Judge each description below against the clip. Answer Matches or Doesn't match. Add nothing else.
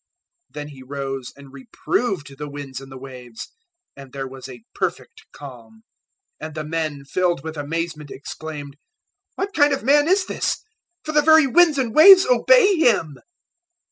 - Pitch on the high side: Doesn't match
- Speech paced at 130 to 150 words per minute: Doesn't match